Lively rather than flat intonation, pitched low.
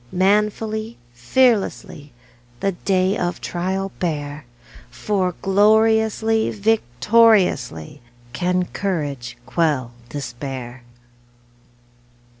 No: wide, 6.7 semitones; medium, 185 Hz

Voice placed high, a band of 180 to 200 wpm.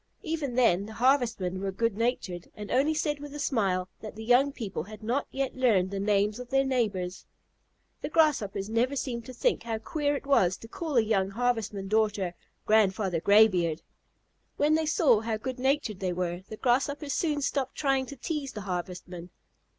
Yes: high, 225 Hz; average, 185 wpm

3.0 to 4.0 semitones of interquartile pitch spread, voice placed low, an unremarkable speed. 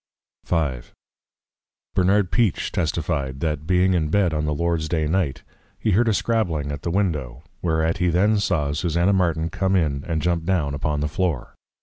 Yes: average, 3.7 semitones; very low, 85 Hz; average, 175 wpm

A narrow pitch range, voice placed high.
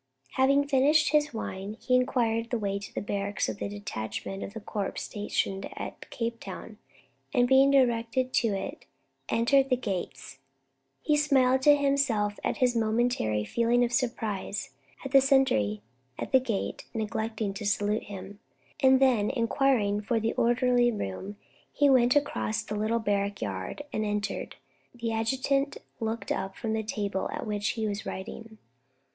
No: average, 4.1 semitones; high, 225 Hz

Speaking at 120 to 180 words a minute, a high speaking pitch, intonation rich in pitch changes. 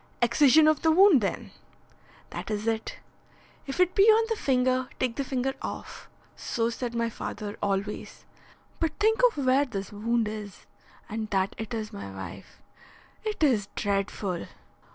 Yes: average, 155 wpm; high, 235 Hz; wide, 5.7 semitones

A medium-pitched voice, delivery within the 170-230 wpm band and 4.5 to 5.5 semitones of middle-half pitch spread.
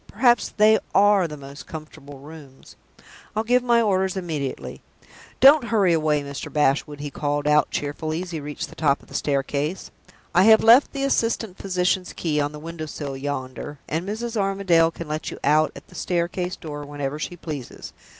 Yes: medium, 160 Hz; average, 180 wpm; average, 5.1 semitones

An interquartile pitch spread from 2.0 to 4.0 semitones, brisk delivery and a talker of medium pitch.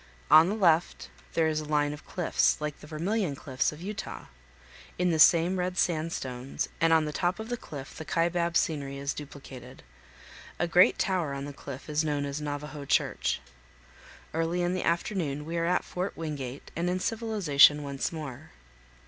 No: average, 3.4 semitones; average, 180 wpm; medium, 155 Hz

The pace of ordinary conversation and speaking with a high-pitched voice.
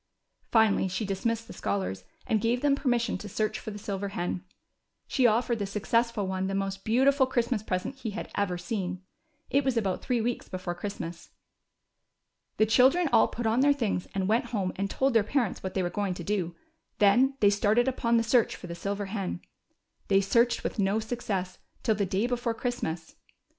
Yes: average, 195 wpm; high, 210 Hz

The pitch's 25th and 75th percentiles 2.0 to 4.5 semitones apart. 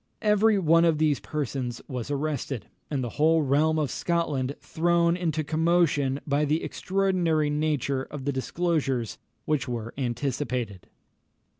Yes: average, 3.8 semitones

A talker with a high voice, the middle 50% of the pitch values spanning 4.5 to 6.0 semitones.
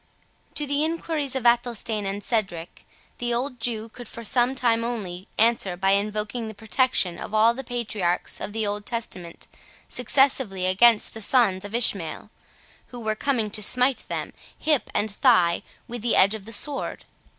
No: high, 225 Hz; average, 3.2 semitones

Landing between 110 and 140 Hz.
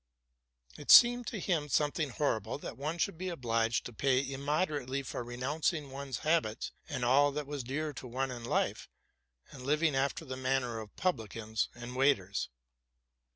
Yes: low, 135 Hz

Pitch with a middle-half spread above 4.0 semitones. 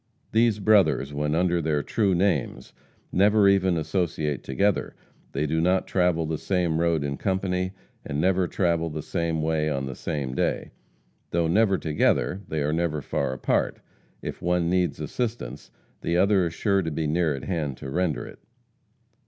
No: average, 3.6 semitones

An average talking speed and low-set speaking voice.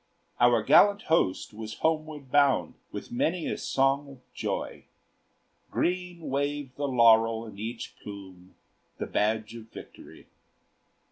No: slow, 125 wpm; low, 125 Hz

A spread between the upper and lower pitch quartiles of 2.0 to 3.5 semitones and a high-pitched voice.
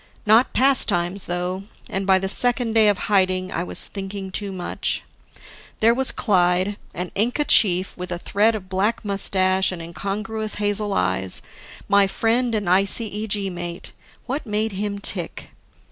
Yes: average, 2.8 semitones; high, 200 Hz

